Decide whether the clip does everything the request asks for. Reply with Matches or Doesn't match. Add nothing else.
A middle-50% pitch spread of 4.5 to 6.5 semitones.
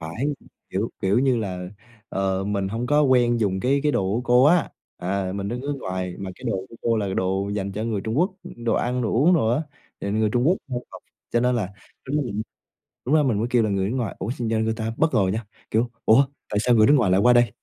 Doesn't match